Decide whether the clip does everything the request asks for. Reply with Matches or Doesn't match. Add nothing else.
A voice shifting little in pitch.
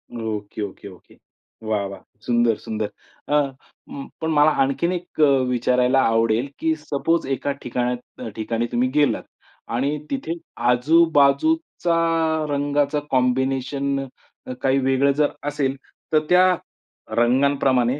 Doesn't match